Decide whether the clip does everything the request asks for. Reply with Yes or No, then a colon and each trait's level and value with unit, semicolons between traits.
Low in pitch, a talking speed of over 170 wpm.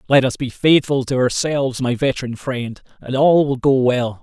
Yes: low, 130 Hz; average, 200 wpm